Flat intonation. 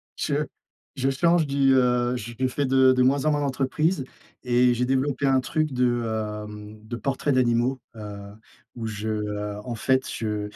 No: average, 3.3 semitones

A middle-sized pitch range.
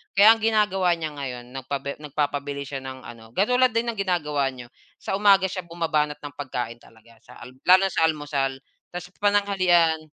No: wide, 6.1 semitones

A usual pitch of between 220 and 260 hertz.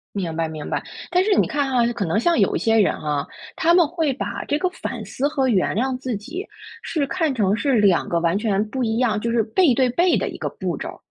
Yes: high, 245 Hz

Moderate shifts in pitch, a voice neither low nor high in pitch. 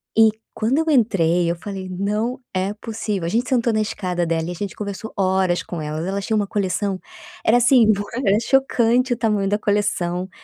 No: average, 3.5 semitones; high, 200 Hz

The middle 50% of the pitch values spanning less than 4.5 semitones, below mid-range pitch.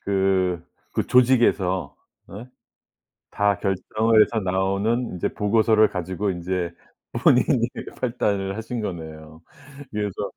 Yes: average, 3.1 semitones; low, 100 Hz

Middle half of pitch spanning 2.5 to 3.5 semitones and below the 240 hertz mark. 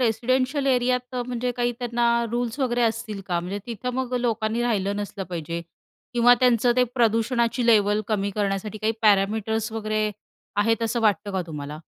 Yes: average, 2.8 semitones; high, 225 Hz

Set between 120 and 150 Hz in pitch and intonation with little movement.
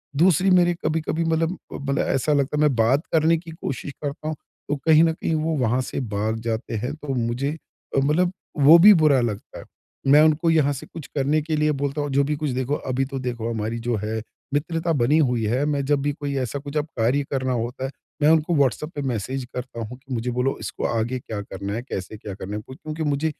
No: medium, 140 Hz; average, 3.9 semitones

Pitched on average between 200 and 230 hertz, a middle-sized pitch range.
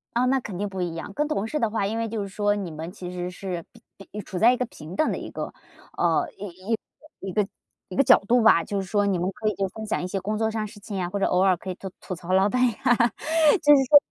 Yes: high, 205 Hz; average, 3.7 semitones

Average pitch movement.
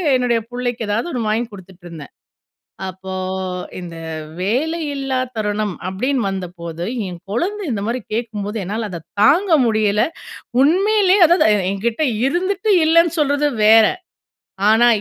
No: wide, 6.8 semitones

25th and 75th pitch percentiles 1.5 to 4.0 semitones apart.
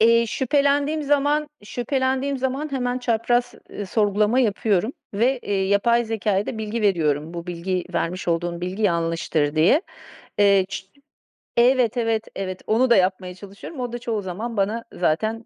No: average, 4.8 semitones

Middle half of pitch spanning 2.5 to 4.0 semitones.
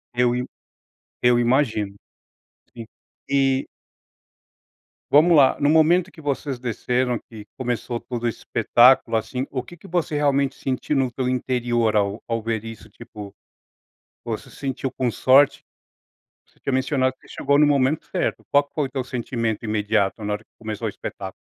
Yes: average, 3.3 semitones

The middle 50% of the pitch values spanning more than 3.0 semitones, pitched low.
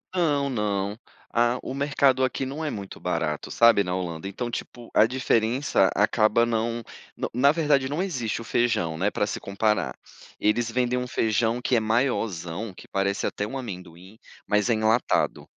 Yes: average, 4.0 semitones; low, 115 Hz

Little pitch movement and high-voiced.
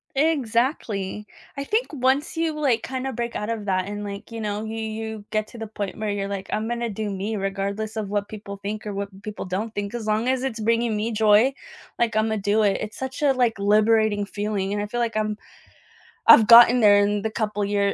Yes: narrow, 2.3 semitones; high, 215 Hz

